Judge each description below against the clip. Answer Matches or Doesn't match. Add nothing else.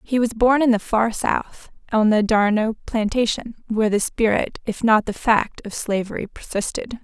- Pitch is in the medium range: Doesn't match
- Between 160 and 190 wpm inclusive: Matches